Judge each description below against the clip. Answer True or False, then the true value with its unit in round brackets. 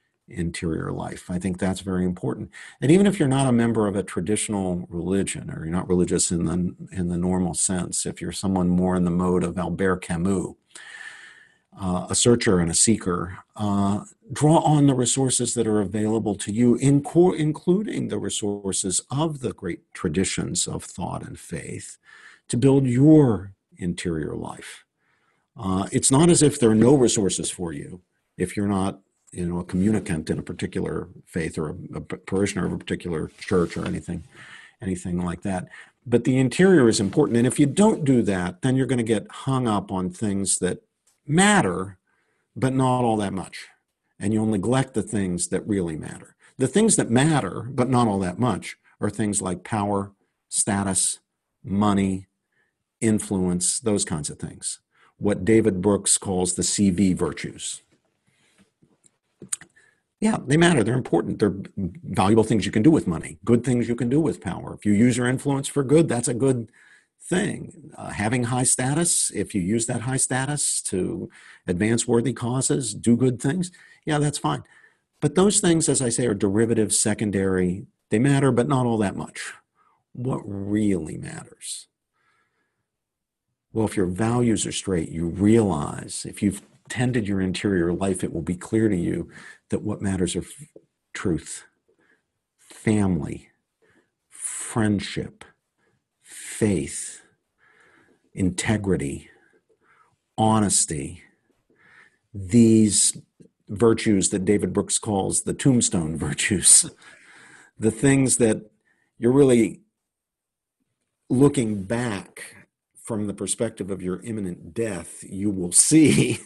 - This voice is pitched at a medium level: False (110 Hz)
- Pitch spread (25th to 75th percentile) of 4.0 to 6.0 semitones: True (4.9 semitones)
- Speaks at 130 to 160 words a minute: True (155 wpm)